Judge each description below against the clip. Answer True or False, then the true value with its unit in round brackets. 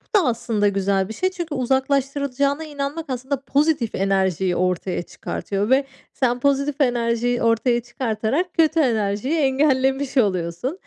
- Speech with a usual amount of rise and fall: True (4.6 semitones)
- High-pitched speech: True (255 Hz)